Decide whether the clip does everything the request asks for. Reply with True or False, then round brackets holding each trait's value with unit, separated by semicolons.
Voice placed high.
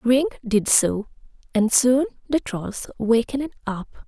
True (245 Hz)